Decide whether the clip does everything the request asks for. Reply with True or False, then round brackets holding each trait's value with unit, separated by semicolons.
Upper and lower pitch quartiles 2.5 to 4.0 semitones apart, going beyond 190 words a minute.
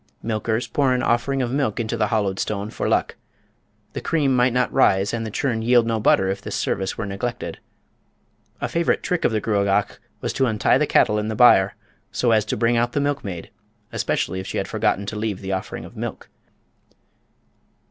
True (3.4 semitones; 200 wpm)